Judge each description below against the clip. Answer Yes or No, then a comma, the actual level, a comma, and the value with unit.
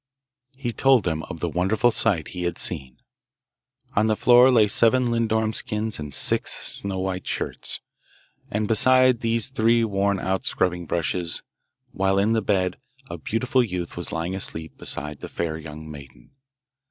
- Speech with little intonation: No, average, 4.7 semitones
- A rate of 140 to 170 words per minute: Yes, average, 160 wpm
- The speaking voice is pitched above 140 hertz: No, low, 100 Hz